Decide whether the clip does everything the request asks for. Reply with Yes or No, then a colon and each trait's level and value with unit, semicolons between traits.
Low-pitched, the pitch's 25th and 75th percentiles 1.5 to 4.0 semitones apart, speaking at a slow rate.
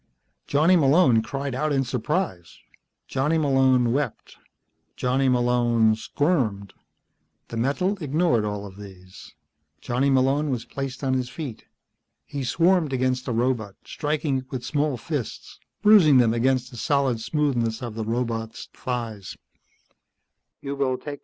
Yes: low, 130 Hz; average, 3.7 semitones; slow, 125 wpm